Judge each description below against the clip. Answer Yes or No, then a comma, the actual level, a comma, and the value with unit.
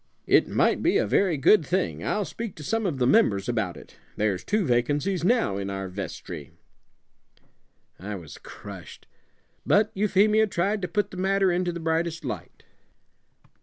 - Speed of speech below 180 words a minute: Yes, average, 165 wpm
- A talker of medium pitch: Yes, medium, 170 Hz